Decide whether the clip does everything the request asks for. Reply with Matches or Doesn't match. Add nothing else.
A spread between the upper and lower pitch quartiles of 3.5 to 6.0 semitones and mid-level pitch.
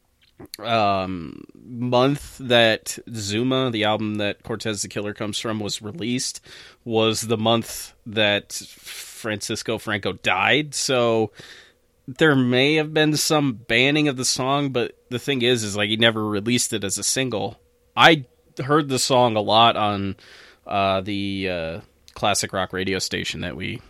Doesn't match